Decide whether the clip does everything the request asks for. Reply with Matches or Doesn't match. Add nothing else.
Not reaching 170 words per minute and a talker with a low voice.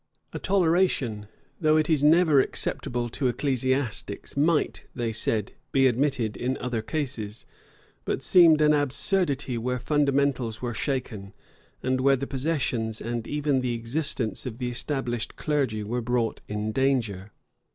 Matches